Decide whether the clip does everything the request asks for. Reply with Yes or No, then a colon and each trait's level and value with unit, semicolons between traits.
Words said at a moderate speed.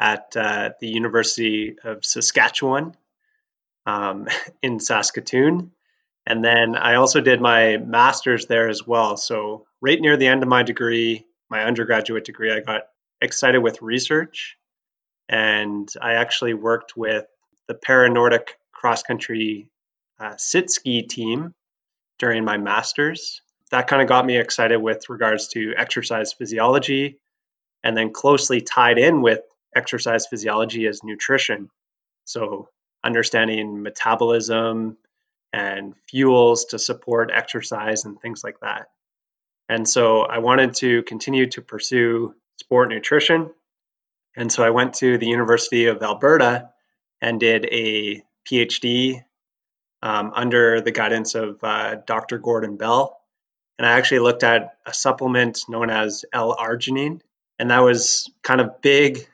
No: slow, 130 wpm